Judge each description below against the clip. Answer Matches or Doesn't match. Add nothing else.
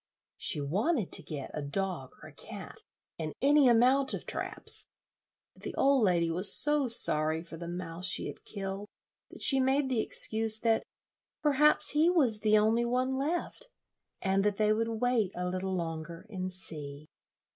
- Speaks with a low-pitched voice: Doesn't match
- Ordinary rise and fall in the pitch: Doesn't match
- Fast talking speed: Doesn't match